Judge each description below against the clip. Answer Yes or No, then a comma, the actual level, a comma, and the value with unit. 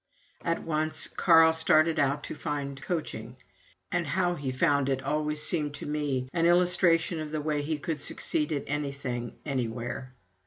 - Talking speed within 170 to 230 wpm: No, average, 160 wpm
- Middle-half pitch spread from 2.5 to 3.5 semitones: Yes, average, 2.8 semitones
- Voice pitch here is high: No, medium, 150 Hz